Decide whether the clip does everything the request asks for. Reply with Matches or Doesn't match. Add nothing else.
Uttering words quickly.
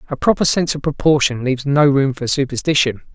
Doesn't match